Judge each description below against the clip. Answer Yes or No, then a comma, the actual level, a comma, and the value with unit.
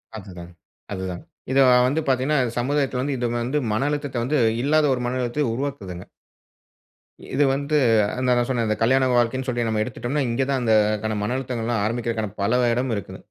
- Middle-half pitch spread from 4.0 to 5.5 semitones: No, average, 3.2 semitones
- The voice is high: No, low, 125 Hz